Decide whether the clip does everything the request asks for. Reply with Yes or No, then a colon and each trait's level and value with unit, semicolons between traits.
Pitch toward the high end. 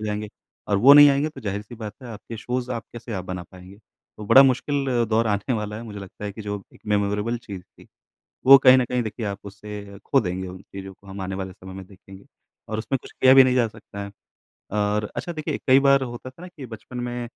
No: low, 105 Hz